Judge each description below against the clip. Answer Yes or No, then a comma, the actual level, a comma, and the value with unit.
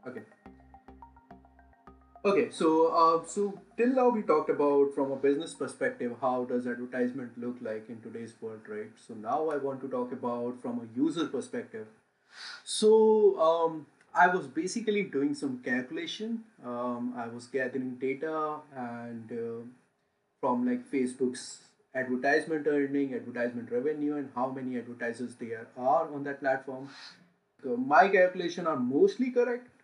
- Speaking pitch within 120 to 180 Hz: Yes, medium, 140 Hz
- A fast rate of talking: No, average, 145 wpm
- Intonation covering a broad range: Yes, wide, 8.5 semitones